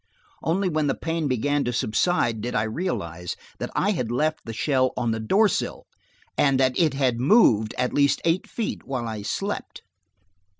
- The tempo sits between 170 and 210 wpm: Yes, average, 180 wpm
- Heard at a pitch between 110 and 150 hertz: Yes, low, 135 Hz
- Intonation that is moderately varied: No, wide, 5.9 semitones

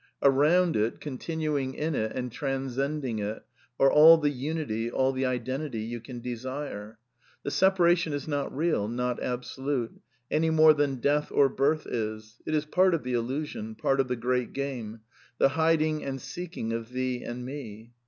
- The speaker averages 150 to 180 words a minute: Yes, average, 175 wpm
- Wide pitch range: No, average, 4.1 semitones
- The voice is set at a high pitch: No, low, 135 Hz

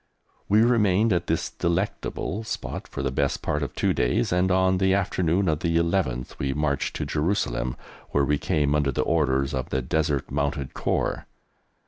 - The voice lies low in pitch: Yes, very low, 80 Hz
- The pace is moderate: Yes, average, 175 wpm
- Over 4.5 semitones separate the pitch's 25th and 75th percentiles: Yes, average, 5.2 semitones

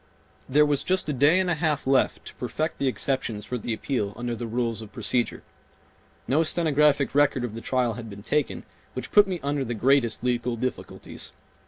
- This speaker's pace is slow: No, average, 195 wpm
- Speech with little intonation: No, average, 3.9 semitones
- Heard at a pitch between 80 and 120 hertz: No, low, 130 Hz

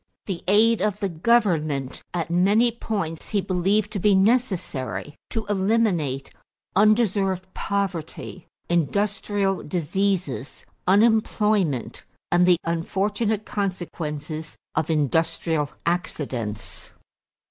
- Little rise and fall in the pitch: No, average, 4.3 semitones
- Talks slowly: Yes, slow, 95 wpm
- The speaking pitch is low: No, high, 190 Hz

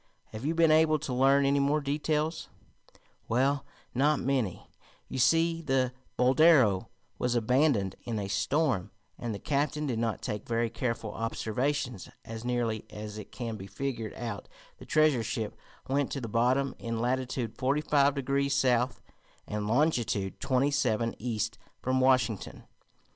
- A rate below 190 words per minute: Yes, average, 150 wpm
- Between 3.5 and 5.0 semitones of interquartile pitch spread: Yes, average, 3.8 semitones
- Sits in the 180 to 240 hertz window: No, low, 125 Hz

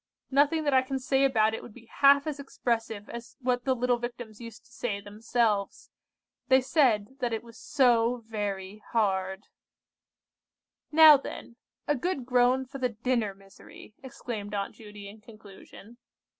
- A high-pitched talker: Yes, high, 235 Hz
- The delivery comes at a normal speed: Yes, average, 155 wpm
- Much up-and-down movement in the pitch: No, average, 3.6 semitones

